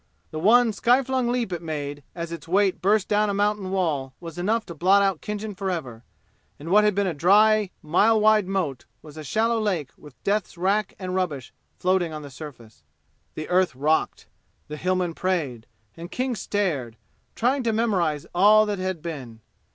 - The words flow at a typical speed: Yes, average, 180 wpm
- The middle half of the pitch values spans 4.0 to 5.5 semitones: Yes, average, 5.2 semitones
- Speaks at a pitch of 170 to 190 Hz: Yes, medium, 185 Hz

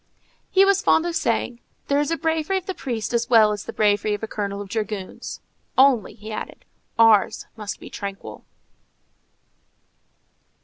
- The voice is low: No, high, 225 Hz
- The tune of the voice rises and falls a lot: Yes, wide, 6.1 semitones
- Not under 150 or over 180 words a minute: Yes, average, 160 wpm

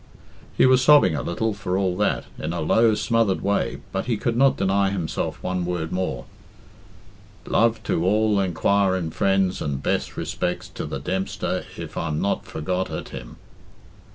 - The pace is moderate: Yes, average, 165 wpm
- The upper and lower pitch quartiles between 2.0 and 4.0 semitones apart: Yes, average, 3.4 semitones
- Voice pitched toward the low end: Yes, very low, 95 Hz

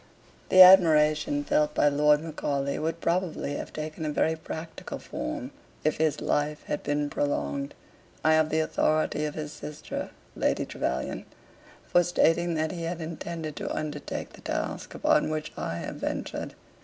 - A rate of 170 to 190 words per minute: No, average, 155 wpm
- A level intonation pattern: Yes, narrow, 1.6 semitones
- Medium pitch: Yes, medium, 155 Hz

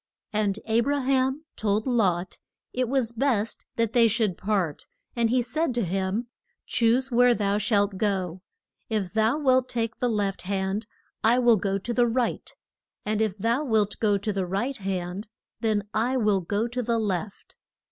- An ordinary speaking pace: Yes, average, 175 wpm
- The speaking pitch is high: Yes, high, 220 Hz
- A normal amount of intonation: Yes, average, 3.3 semitones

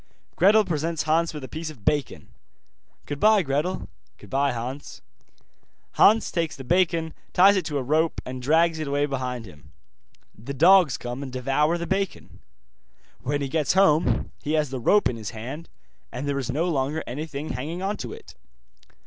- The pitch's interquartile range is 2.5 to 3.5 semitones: No, average, 4.1 semitones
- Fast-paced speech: No, average, 175 wpm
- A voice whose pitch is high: No, medium, 150 Hz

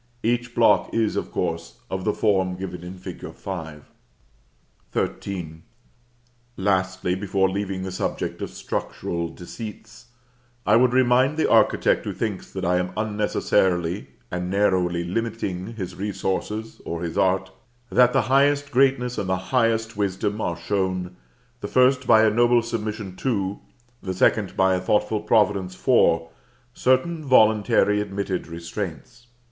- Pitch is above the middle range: No, low, 100 Hz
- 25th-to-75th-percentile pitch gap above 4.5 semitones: No, average, 3.7 semitones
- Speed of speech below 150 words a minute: Yes, average, 140 wpm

